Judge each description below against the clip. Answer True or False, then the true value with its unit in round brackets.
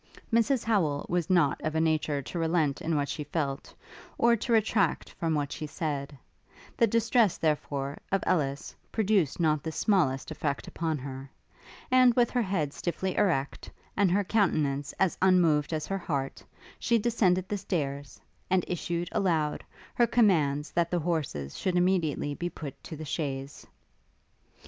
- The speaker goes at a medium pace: True (160 wpm)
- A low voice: False (165 Hz)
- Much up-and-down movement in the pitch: False (4.8 semitones)